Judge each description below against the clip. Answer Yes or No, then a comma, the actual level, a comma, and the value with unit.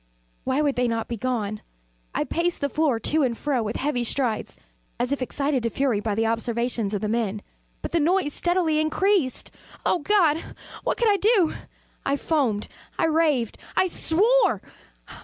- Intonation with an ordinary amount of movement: No, wide, 5.8 semitones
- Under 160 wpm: No, average, 175 wpm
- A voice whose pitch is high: Yes, very high, 275 Hz